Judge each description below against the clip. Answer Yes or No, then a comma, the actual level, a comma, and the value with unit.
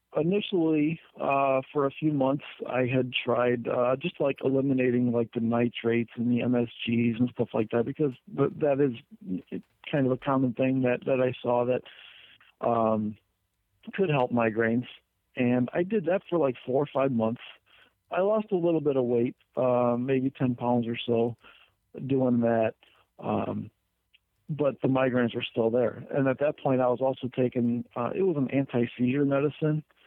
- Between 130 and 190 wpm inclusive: Yes, average, 170 wpm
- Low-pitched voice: Yes, low, 125 Hz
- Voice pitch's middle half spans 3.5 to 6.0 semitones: No, average, 2.7 semitones